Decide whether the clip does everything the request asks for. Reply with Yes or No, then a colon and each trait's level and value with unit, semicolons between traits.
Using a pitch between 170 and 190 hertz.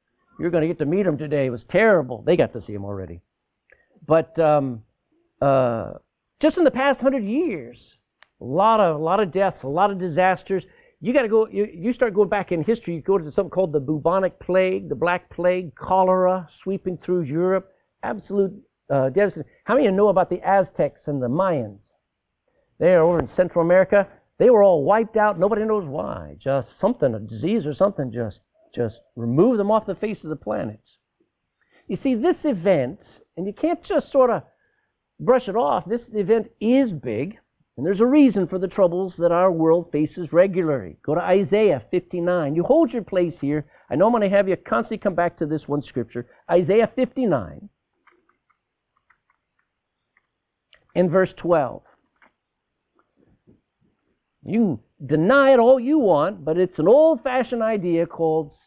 Yes: medium, 185 Hz